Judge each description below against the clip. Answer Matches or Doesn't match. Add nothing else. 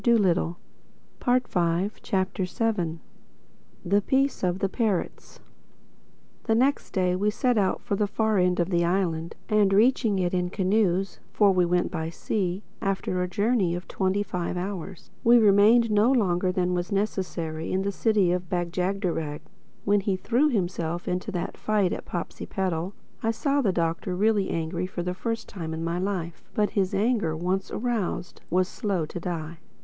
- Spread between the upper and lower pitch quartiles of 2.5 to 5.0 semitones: Matches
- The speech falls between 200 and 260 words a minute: Doesn't match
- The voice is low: Doesn't match